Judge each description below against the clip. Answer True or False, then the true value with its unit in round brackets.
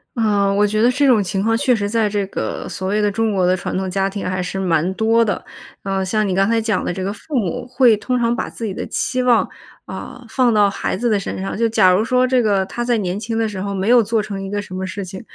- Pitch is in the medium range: False (210 Hz)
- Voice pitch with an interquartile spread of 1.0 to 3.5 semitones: True (3.1 semitones)